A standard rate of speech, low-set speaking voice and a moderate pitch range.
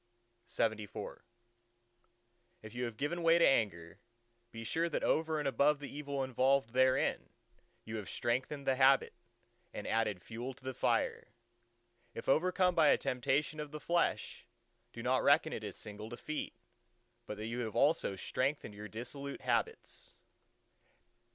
Yes: average, 150 wpm; low, 130 Hz; average, 4.6 semitones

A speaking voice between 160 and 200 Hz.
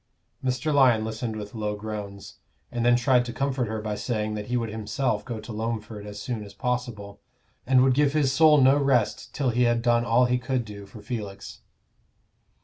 No: low, 120 Hz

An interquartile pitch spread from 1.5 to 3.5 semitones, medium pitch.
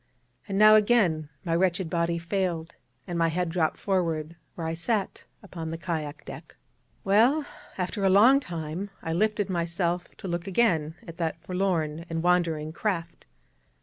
Yes: average, 2.9 semitones; medium, 175 Hz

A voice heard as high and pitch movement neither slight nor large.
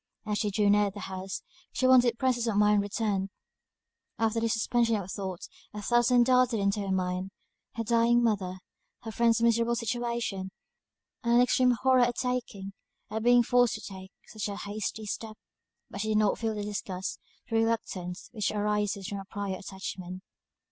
Yes: high, 215 Hz; average, 3.0 semitones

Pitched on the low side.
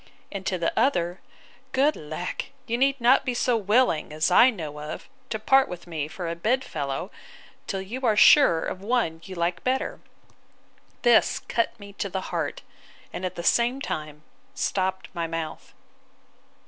No: high, 190 Hz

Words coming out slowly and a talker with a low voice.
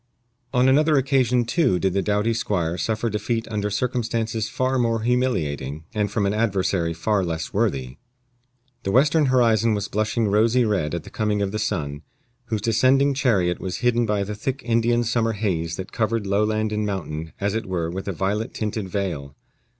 No: average, 180 wpm; low, 105 Hz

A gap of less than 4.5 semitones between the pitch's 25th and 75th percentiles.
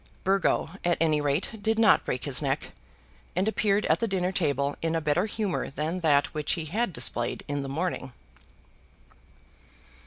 No: average, 5.0 semitones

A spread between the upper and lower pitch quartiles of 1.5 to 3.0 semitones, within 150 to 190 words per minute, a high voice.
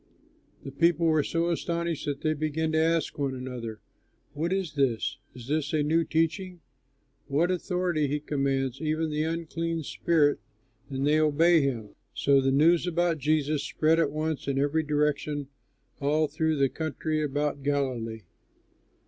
No: narrow, 2.6 semitones; average, 155 wpm; medium, 155 Hz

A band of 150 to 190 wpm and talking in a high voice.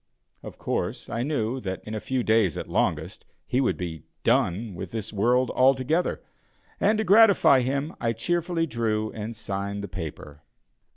No: average, 165 wpm; low, 115 Hz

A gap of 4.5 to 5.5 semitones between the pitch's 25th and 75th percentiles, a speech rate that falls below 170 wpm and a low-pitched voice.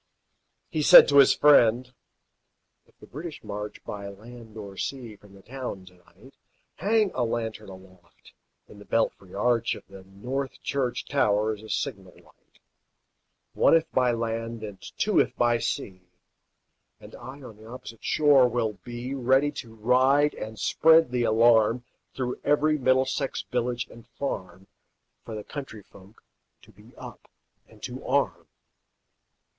No: average, 3.9 semitones; average, 150 wpm; low, 120 Hz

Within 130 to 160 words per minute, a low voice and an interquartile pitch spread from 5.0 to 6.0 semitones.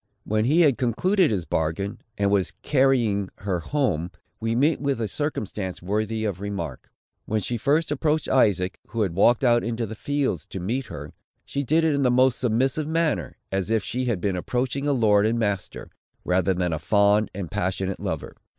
No: average, 190 wpm; low, 110 Hz; wide, 5.5 semitones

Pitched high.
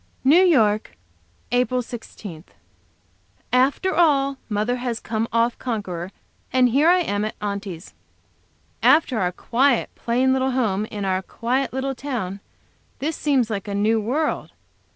Yes: high, 240 Hz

